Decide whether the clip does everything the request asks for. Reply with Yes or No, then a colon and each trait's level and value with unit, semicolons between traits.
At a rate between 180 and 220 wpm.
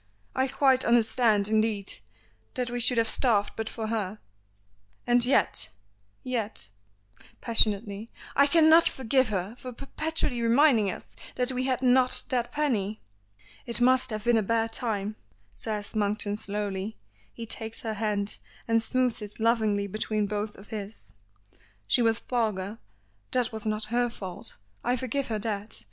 No: average, 150 wpm